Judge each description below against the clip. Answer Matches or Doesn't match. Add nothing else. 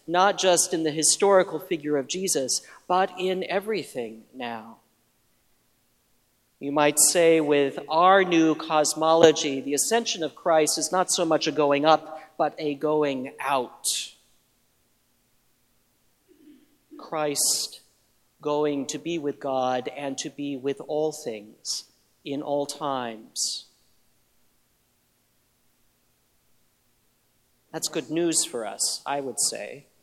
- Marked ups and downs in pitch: Doesn't match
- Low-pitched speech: Doesn't match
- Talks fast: Doesn't match